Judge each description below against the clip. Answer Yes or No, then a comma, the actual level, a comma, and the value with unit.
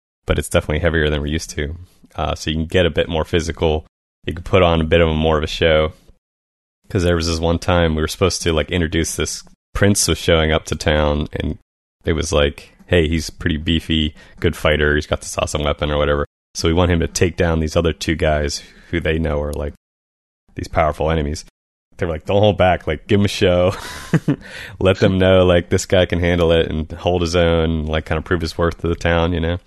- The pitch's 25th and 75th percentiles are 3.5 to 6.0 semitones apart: No, narrow, 2.5 semitones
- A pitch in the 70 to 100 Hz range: Yes, very low, 80 Hz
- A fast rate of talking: Yes, fast, 245 wpm